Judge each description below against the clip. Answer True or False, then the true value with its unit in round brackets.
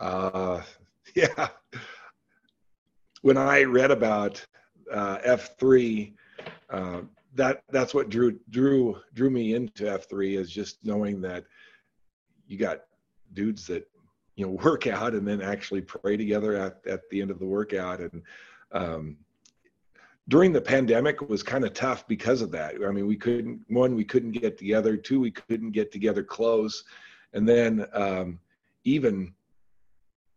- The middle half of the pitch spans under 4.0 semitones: True (3.4 semitones)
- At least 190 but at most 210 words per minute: False (150 wpm)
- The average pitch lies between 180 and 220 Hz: False (105 Hz)